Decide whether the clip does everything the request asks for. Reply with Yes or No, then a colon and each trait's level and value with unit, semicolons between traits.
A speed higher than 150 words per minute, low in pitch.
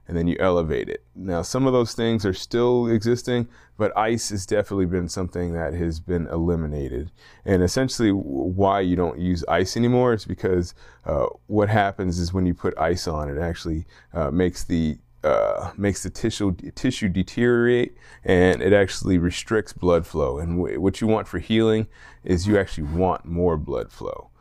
Yes: average, 185 wpm; very low, 95 Hz